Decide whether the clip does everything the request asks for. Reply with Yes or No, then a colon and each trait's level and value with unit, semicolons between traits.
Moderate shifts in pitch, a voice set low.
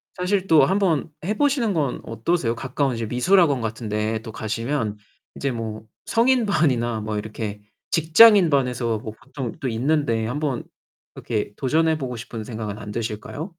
No: wide, 6.4 semitones; low, 125 Hz